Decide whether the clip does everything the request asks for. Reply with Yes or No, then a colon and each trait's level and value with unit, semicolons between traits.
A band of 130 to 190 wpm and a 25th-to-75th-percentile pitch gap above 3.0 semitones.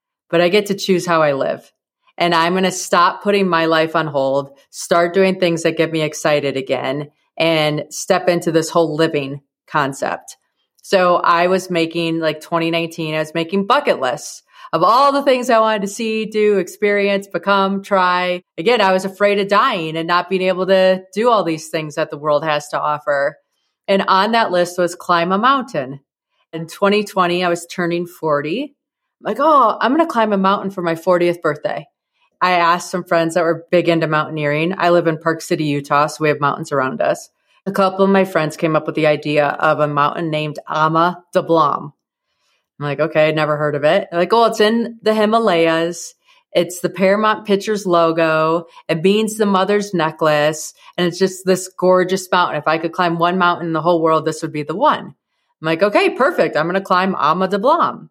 No: fast, 205 wpm; average, 3.6 semitones